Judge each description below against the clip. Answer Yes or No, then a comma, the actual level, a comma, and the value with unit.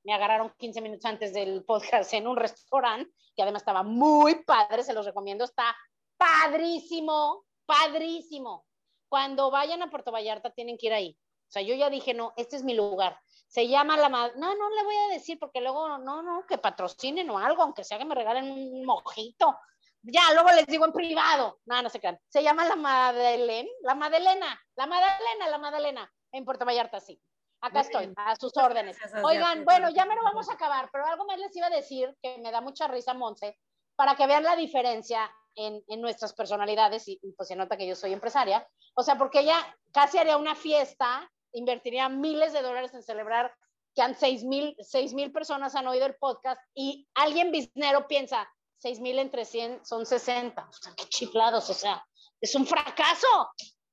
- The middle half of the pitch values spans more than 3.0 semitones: Yes, average, 4.9 semitones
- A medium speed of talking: No, fast, 195 wpm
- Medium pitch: No, very high, 265 Hz